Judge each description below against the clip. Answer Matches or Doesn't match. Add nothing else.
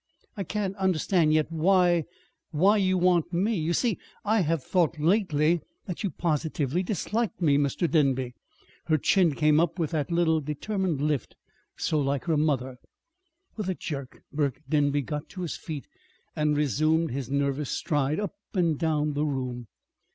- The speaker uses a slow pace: Doesn't match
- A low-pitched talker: Doesn't match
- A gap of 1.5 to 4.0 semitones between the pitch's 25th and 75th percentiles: Matches